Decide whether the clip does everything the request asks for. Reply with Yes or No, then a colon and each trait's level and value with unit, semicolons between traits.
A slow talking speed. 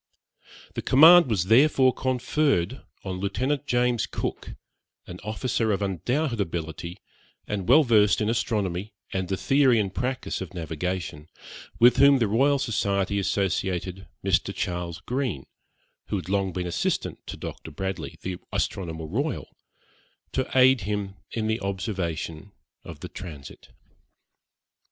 Yes: slow, 130 wpm